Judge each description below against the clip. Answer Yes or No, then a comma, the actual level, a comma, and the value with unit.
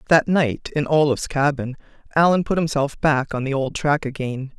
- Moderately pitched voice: Yes, medium, 145 Hz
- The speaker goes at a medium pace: Yes, average, 185 wpm